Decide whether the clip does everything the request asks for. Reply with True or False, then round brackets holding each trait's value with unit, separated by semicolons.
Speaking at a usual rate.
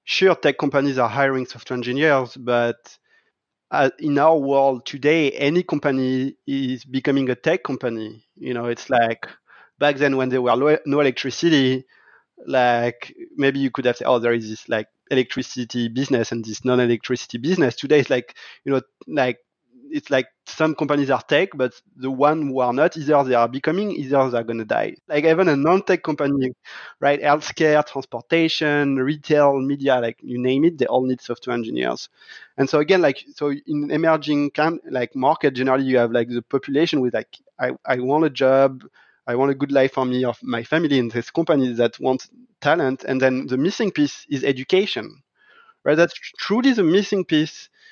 True (180 wpm)